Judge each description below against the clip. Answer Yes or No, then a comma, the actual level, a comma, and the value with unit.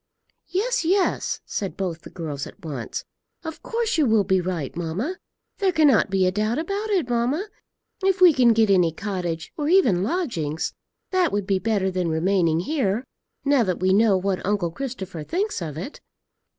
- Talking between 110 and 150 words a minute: No, average, 175 wpm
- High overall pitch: Yes, high, 205 Hz